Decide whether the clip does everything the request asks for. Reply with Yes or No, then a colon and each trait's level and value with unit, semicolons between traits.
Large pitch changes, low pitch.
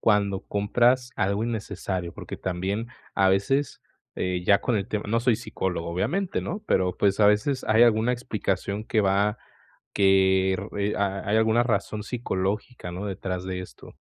No: average, 2.9 semitones; low, 100 Hz